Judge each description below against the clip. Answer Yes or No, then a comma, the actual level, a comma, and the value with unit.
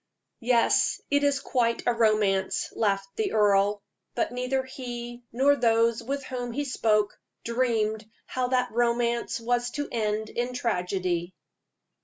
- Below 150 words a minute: Yes, average, 140 wpm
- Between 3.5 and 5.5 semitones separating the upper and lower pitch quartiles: No, average, 2.7 semitones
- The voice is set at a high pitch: Yes, high, 235 Hz